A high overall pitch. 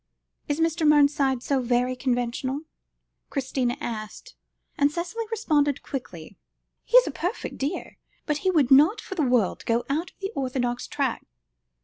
Yes: very high, 280 Hz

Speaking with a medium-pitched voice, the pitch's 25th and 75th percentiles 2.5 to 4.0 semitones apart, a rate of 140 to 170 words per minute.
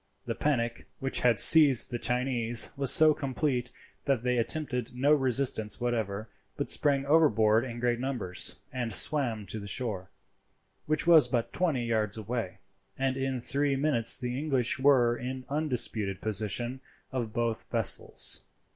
No: low, 125 Hz; average, 3.1 semitones; average, 145 wpm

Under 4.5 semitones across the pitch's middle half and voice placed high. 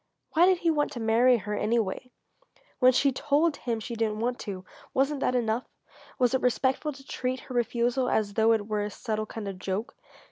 Yes: average, 3.4 semitones; high, 240 Hz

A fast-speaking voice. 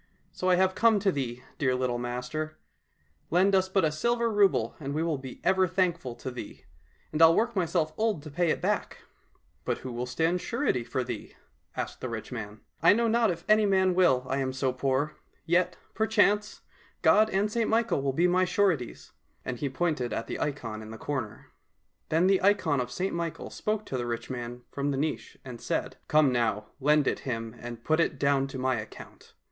Yes: fast, 220 wpm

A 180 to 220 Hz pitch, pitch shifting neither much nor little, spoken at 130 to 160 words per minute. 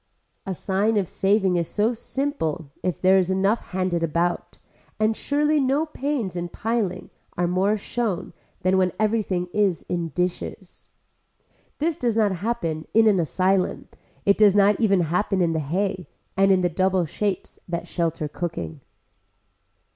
Yes: high, 190 Hz; average, 3.5 semitones; average, 155 wpm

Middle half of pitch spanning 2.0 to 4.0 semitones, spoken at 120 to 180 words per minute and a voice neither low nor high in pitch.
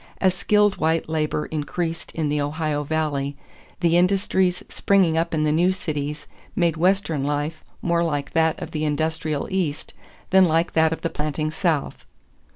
Yes: narrow, 2.6 semitones; average, 160 wpm; medium, 160 Hz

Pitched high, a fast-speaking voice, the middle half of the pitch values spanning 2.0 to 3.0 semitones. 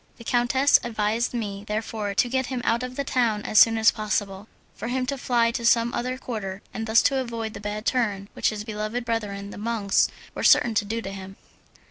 Yes: high, 225 Hz; fast, 210 wpm; narrow, 2.6 semitones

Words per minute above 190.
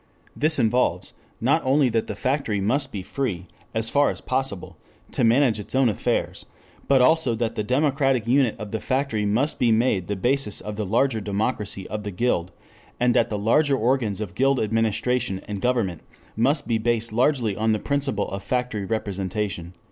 No: average, 180 wpm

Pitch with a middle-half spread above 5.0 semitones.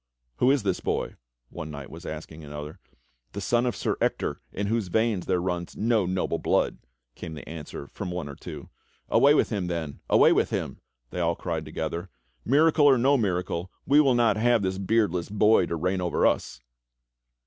Yes: wide, 5.4 semitones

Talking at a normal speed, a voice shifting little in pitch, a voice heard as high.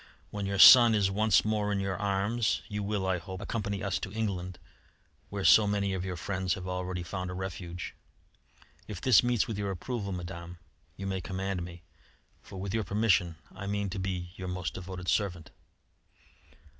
No: average, 180 wpm; narrow, 2.1 semitones; very low, 95 Hz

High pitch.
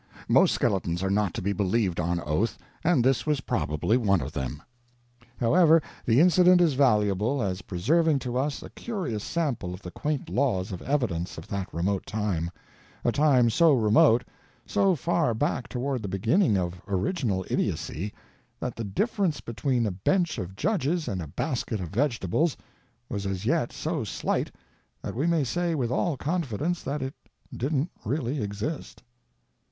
No: low, 120 Hz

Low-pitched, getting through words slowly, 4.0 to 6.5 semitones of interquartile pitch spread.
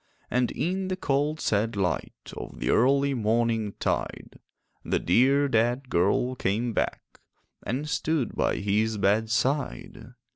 Yes: low, 120 Hz; slow, 120 wpm; average, 4.3 semitones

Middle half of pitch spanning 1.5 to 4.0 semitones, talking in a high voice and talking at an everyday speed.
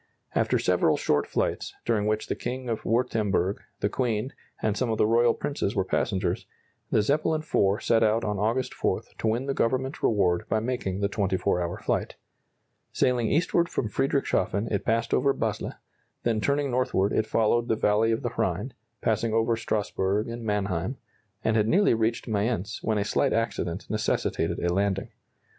No: average, 3.0 semitones; low, 110 Hz; average, 175 wpm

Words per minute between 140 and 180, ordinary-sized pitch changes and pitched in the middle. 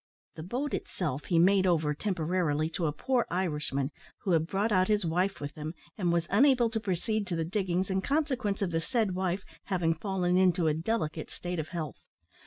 No: average, 195 wpm; average, 3.6 semitones; medium, 180 Hz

